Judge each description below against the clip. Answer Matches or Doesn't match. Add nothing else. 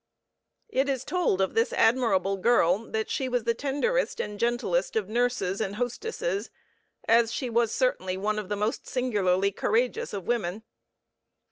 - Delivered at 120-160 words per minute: Matches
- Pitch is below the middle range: Doesn't match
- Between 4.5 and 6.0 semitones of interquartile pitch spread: Doesn't match